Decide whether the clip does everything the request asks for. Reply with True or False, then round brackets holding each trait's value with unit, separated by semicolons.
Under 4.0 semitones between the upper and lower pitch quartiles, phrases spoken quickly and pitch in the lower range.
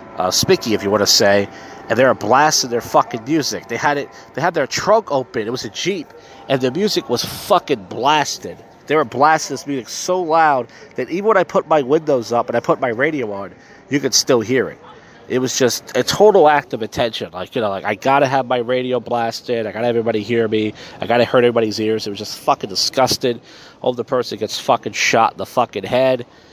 True (3.3 semitones; 230 wpm; 125 Hz)